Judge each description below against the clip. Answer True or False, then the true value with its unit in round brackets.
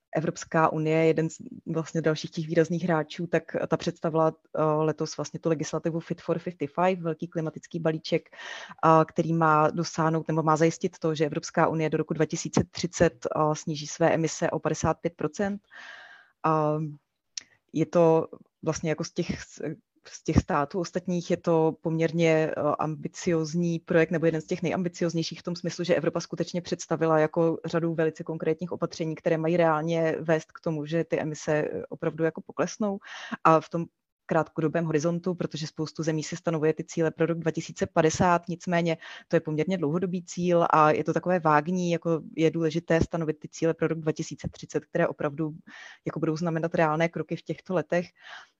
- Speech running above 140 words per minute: True (165 wpm)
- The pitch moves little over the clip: True (1.3 semitones)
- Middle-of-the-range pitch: True (165 Hz)